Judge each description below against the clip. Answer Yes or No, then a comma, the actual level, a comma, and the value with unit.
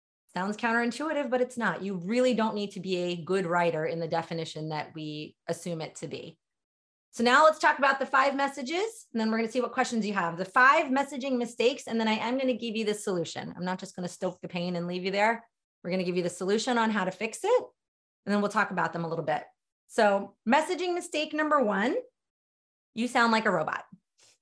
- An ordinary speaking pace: No, fast, 240 wpm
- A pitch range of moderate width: No, wide, 6.1 semitones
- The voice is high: Yes, high, 220 Hz